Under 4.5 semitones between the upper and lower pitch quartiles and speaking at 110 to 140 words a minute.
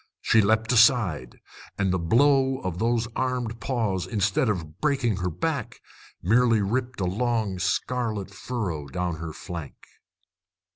No: average, 4.9 semitones; slow, 135 wpm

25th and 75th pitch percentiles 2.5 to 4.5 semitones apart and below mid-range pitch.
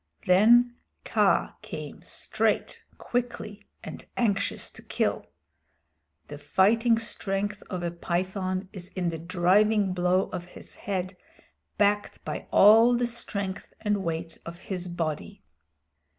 No: average, 3.1 semitones; high, 195 Hz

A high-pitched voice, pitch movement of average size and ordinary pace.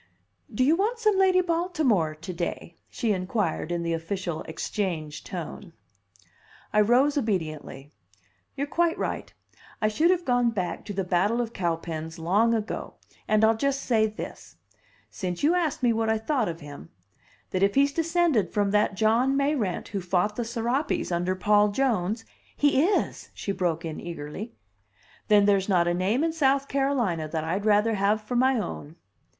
No: high, 210 Hz; wide, 7.1 semitones; average, 170 wpm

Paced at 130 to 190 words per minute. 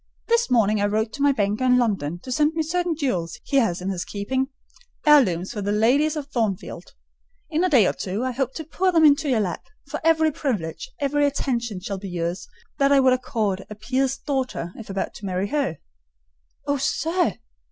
No: average, 200 wpm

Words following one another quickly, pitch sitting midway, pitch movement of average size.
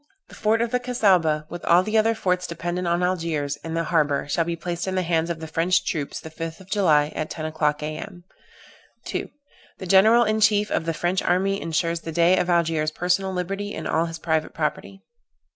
Yes: fast, 210 wpm; medium, 170 Hz; average, 3.0 semitones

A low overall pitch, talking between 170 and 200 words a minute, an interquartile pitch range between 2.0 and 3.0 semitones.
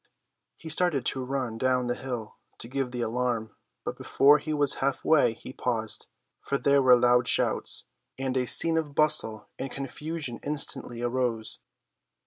No: low, 130 Hz; average, 160 wpm; average, 2.7 semitones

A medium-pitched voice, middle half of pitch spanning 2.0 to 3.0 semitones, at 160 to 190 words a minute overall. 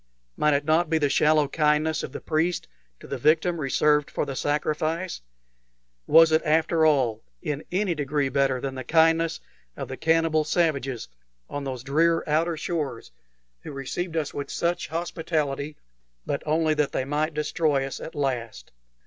Yes: medium, 150 Hz; average, 2.7 semitones; average, 165 wpm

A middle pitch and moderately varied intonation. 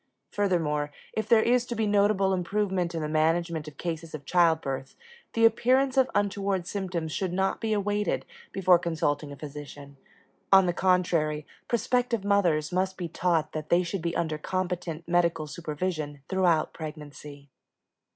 Yes: medium, 175 Hz; average, 4.1 semitones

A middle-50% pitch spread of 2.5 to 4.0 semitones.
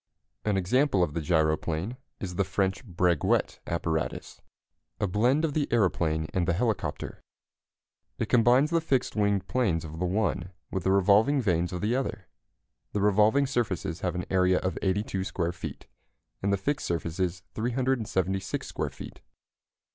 No: average, 4.6 semitones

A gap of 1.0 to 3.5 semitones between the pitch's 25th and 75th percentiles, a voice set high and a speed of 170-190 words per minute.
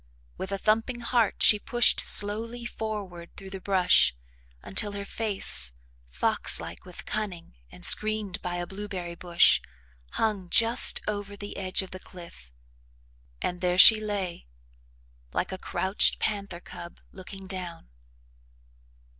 No: average, 3.1 semitones; high, 195 Hz; slow, 135 wpm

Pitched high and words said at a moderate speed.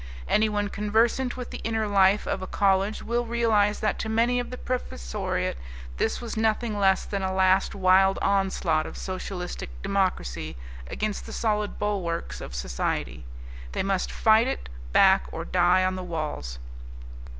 Yes: high, 195 Hz; average, 155 wpm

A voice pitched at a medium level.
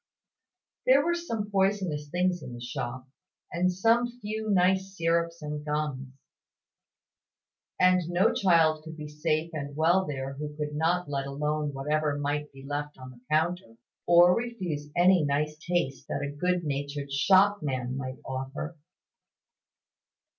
Yes: medium, 155 Hz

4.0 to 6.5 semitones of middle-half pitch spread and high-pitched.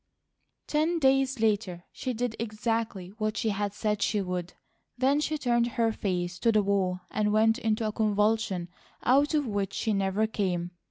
No: average, 3.1 semitones; high, 215 Hz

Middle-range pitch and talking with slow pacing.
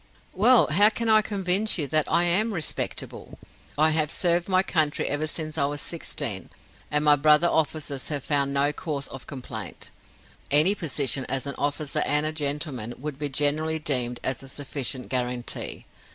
No: medium, 150 Hz; average, 165 wpm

